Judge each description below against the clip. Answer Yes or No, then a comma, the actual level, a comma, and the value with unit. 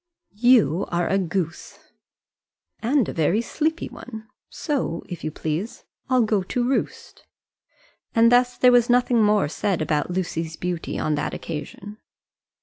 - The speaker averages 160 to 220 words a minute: No, average, 145 wpm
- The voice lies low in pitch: No, high, 205 Hz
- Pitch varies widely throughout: Yes, wide, 6.6 semitones